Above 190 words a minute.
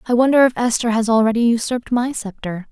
Yes: average, 200 wpm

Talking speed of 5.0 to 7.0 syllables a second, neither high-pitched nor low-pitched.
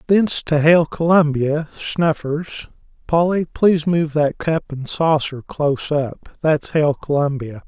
No: 4.1 syllables/s; medium, 155 Hz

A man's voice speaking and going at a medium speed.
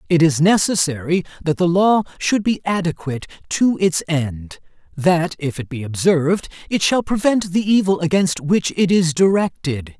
Yes: male; average, 160 wpm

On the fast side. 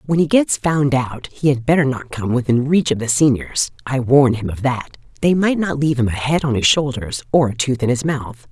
Yes: fast, 255 wpm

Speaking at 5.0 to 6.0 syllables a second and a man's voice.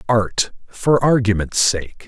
No: 3.4 syllables/s; male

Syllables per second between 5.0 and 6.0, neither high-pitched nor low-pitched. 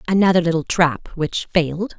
Yes: 5.1 syllables/s; medium, 170 Hz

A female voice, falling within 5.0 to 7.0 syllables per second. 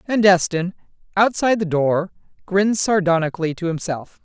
Yes: female; 5.4 syllables/s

